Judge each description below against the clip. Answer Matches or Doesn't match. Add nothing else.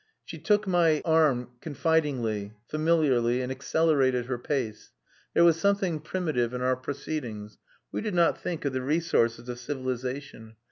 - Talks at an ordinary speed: Matches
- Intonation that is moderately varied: Matches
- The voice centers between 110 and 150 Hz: Matches